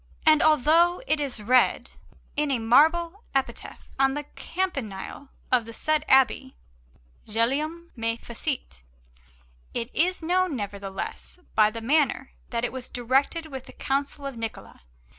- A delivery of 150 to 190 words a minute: No, average, 140 wpm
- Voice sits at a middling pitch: No, very high, 270 Hz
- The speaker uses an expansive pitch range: No, average, 5.0 semitones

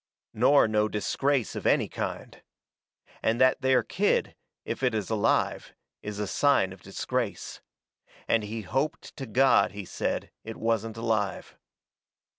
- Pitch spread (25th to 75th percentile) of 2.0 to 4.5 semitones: Yes, average, 3.5 semitones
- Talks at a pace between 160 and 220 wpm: No, average, 140 wpm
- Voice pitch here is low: Yes, low, 110 Hz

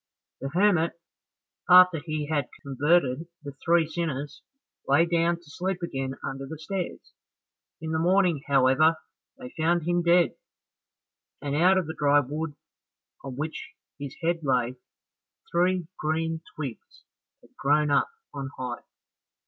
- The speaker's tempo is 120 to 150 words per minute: Yes, slow, 135 wpm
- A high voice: No, medium, 160 Hz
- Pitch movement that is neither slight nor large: Yes, average, 3.3 semitones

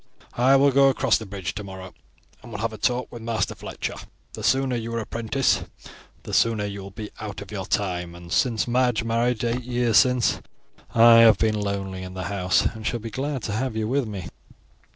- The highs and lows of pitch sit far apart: No, average, 3.5 semitones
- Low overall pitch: Yes, low, 110 Hz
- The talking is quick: Yes, fast, 210 wpm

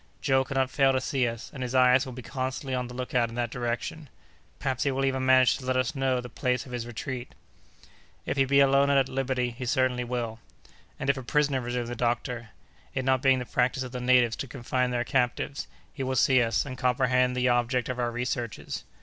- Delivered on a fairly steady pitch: Yes, narrow, 1.4 semitones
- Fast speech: Yes, fast, 225 wpm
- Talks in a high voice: No, low, 125 Hz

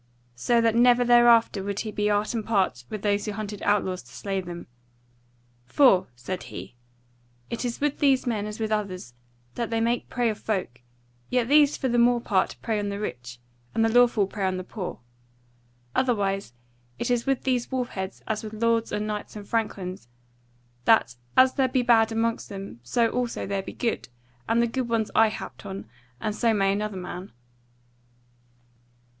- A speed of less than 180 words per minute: No, average, 185 wpm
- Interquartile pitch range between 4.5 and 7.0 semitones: No, average, 3.3 semitones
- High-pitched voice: Yes, high, 215 Hz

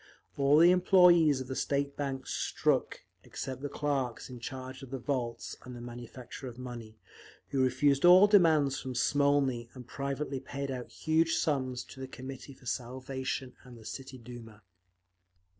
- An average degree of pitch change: No, narrow, 2.2 semitones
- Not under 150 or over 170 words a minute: Yes, average, 160 wpm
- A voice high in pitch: No, low, 130 Hz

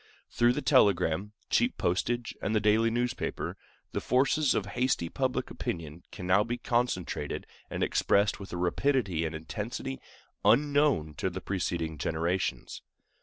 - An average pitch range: No, wide, 5.9 semitones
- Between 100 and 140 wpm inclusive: Yes, slow, 135 wpm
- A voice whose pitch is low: Yes, low, 105 Hz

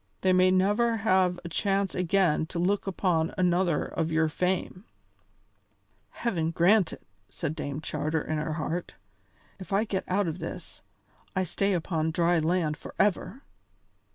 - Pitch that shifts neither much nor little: Yes, average, 3.0 semitones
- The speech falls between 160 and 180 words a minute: No, average, 150 wpm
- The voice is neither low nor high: Yes, medium, 180 Hz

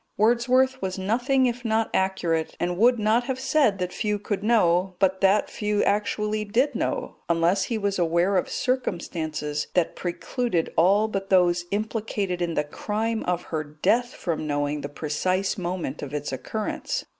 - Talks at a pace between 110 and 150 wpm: No, average, 165 wpm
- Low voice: No, high, 195 Hz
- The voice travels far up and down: No, average, 4.3 semitones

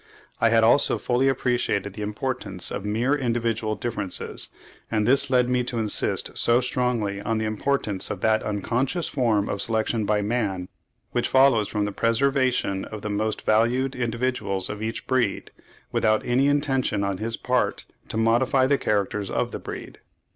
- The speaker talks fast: No, average, 165 wpm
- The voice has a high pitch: No, low, 115 Hz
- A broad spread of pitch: No, average, 3.2 semitones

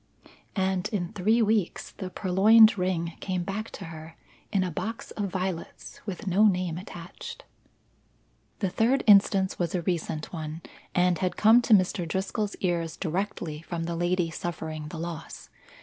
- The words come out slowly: No, average, 155 wpm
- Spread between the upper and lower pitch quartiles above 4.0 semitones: No, average, 3.1 semitones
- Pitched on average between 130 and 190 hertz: Yes, medium, 185 Hz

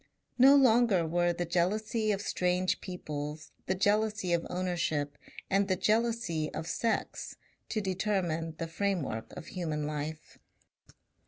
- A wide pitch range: No, average, 4.5 semitones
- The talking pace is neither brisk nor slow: No, slow, 130 wpm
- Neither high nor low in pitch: Yes, medium, 180 Hz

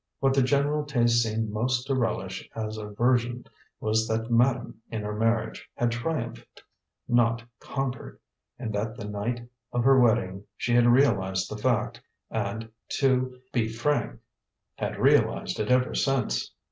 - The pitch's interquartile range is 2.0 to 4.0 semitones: Yes, average, 2.7 semitones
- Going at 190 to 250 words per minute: No, average, 150 wpm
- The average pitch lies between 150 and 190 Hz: No, low, 115 Hz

